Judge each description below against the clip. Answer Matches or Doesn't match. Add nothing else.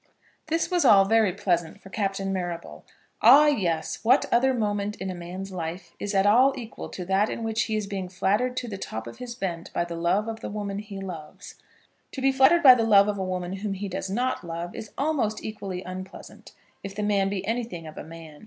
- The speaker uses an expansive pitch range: Doesn't match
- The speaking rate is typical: Doesn't match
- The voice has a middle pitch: Doesn't match